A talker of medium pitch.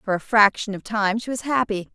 No: high, 210 Hz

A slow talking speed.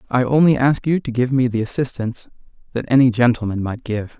No: average, 200 wpm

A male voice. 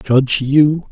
Yes: male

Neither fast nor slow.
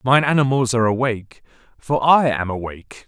Yes: average, 155 wpm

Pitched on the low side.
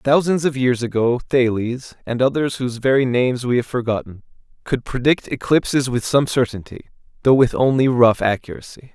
Yes: low, 125 Hz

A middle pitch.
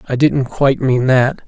No: low, 130 Hz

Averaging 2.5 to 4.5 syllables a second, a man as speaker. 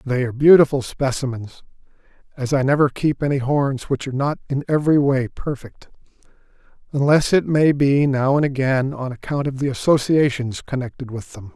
No: 5.3 syllables/s; male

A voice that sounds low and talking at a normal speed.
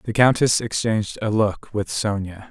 Yes: low, 105 Hz; average, 170 wpm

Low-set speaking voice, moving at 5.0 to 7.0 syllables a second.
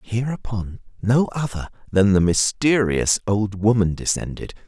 No: low, 105 Hz; 4.3 syllables/s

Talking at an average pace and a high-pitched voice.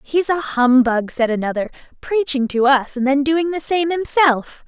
Yes: average, 180 wpm; very high, 280 Hz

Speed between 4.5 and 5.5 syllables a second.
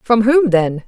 No: 3.9 syllables/s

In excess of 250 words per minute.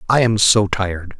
No: average, 200 wpm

